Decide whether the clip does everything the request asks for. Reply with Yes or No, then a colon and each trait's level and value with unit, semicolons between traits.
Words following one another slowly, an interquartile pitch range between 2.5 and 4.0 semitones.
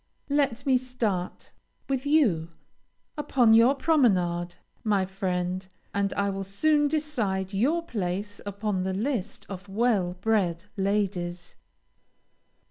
No: slow, 115 wpm; average, 5.3 semitones